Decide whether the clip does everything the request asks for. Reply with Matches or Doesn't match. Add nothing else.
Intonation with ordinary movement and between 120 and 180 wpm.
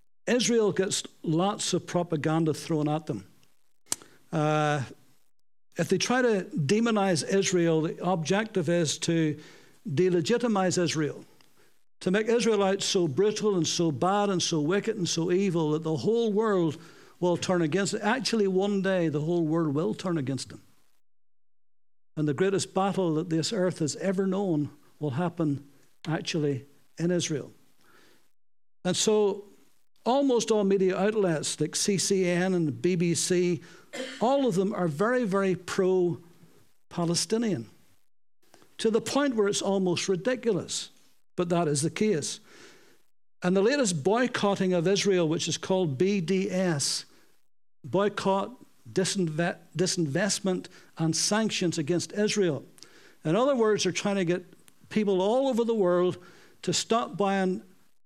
Matches